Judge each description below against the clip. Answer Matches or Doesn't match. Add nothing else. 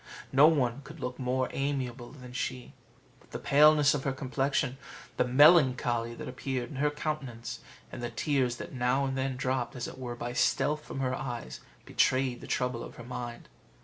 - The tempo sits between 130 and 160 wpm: Doesn't match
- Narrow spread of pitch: Matches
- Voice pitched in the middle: Doesn't match